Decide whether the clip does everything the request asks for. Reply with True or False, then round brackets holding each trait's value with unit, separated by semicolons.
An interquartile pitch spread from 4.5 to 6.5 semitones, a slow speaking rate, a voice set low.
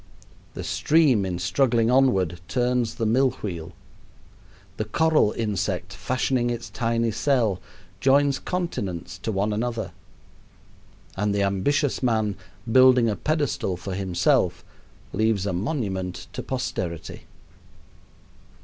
True (5.2 semitones; 115 wpm; 110 Hz)